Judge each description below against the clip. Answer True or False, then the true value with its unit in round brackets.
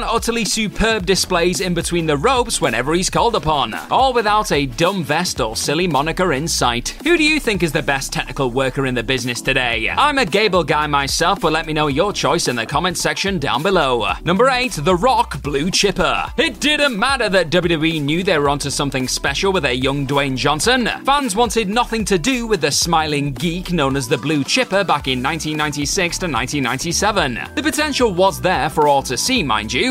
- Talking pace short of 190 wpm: False (205 wpm)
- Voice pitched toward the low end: False (170 Hz)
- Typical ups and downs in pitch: False (6.7 semitones)